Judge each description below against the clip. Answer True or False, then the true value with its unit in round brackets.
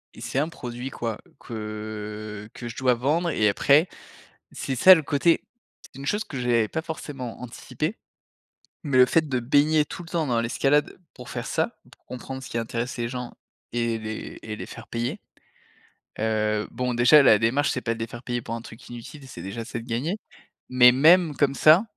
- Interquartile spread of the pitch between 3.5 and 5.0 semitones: True (3.9 semitones)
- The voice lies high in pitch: False (125 Hz)